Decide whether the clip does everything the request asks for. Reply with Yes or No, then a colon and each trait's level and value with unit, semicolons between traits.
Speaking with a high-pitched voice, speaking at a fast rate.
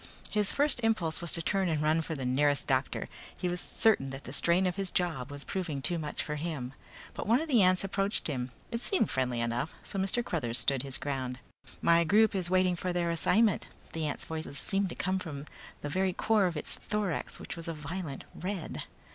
No: medium, 170 Hz; fast, 220 wpm